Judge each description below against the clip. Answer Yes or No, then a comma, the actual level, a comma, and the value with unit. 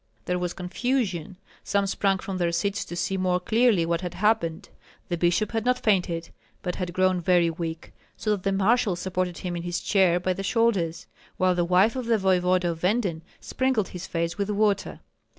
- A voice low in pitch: No, medium, 185 Hz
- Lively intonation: No, average, 2.7 semitones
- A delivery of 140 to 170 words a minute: No, average, 195 wpm